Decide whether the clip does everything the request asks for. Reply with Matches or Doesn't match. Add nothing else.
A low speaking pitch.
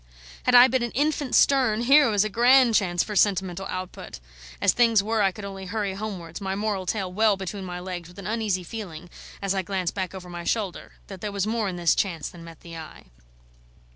Doesn't match